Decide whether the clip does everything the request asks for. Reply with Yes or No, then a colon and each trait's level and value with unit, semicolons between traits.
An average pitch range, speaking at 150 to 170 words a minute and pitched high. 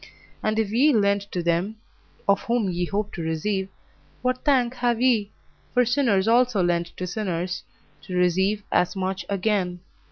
Yes: average, 4.1 semitones; average, 160 wpm; high, 200 Hz